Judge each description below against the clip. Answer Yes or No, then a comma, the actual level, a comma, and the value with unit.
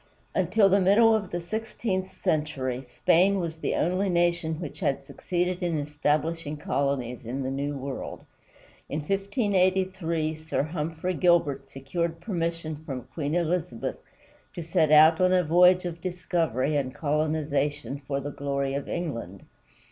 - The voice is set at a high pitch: No, medium, 160 Hz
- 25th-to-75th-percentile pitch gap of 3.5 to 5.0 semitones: Yes, average, 4.0 semitones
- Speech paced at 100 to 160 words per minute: Yes, average, 140 wpm